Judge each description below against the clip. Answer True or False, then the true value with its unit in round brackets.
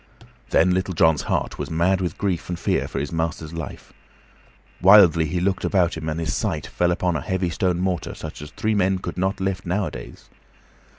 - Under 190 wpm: False (195 wpm)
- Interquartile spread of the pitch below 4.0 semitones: True (2.6 semitones)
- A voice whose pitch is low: True (90 Hz)